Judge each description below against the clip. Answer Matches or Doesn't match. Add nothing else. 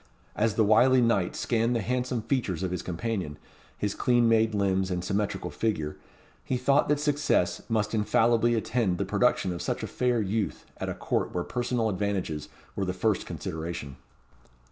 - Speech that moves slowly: Doesn't match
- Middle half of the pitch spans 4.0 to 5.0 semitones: Matches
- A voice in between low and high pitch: Doesn't match